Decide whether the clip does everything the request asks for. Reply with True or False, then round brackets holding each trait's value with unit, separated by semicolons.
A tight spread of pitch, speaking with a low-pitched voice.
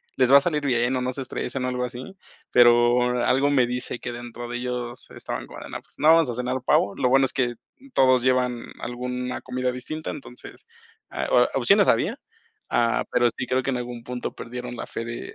True (1.1 semitones; 125 Hz)